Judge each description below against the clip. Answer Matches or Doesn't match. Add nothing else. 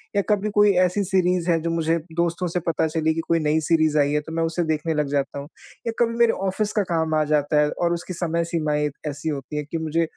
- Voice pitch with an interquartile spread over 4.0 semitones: Doesn't match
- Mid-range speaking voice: Matches